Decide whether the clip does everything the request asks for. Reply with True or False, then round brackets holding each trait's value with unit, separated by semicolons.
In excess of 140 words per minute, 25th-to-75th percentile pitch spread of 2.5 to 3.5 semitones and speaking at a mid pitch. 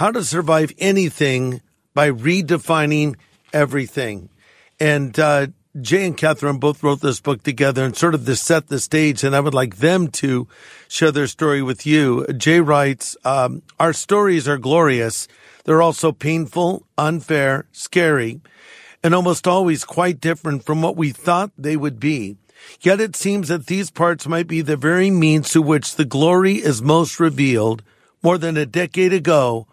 True (165 wpm; 3.2 semitones; 155 Hz)